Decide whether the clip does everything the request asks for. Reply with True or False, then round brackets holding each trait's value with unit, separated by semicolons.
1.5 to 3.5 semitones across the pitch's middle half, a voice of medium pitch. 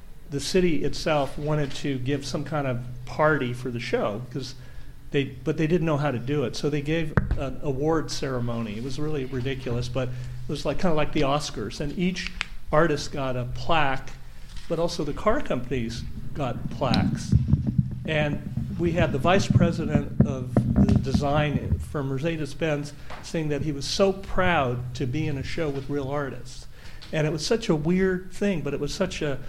True (3.2 semitones; 145 Hz)